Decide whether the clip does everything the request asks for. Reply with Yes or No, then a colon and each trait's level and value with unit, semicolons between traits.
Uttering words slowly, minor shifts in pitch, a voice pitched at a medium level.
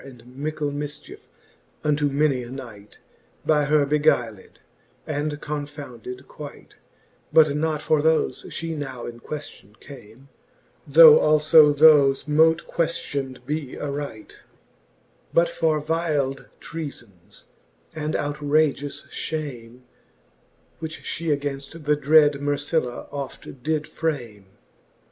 Yes: slow, 110 wpm; narrow, 2.2 semitones; medium, 145 Hz